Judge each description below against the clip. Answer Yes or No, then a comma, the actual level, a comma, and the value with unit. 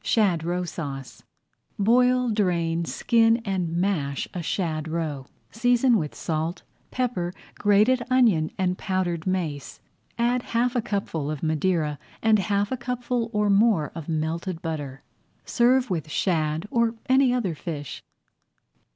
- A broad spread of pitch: Yes, wide, 6.3 semitones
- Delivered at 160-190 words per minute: No, slow, 135 wpm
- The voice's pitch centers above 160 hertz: Yes, medium, 185 Hz